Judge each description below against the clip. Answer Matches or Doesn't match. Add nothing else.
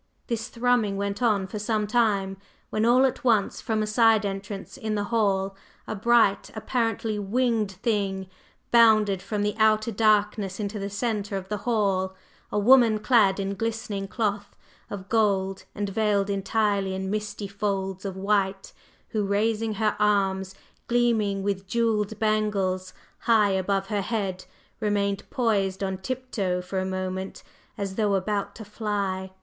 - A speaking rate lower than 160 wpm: Matches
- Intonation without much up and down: Matches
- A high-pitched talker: Matches